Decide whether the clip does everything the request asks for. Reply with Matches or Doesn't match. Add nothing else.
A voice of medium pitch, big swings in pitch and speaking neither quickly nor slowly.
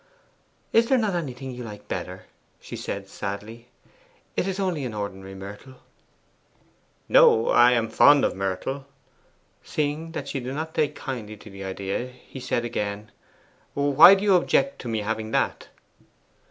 Doesn't match